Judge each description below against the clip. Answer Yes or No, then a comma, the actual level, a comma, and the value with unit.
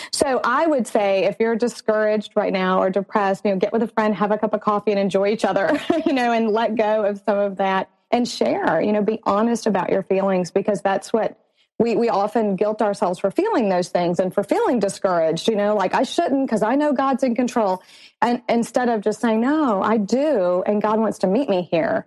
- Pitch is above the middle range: Yes, high, 215 Hz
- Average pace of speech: No, fast, 235 wpm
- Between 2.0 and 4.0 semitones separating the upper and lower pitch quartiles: Yes, average, 2.9 semitones